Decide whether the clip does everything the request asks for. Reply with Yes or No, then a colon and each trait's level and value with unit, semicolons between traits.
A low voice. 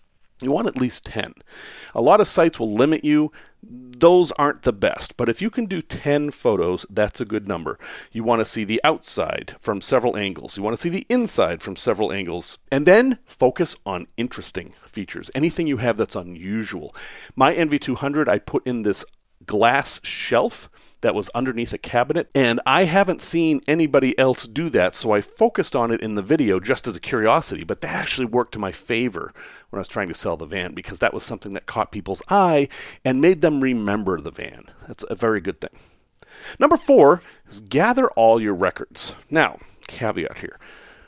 Yes: low, 130 Hz